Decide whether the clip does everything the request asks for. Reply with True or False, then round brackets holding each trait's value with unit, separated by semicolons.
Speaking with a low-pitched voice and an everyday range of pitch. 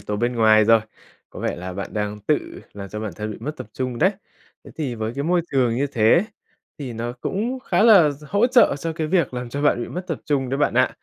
False (130 Hz; 6.5 semitones)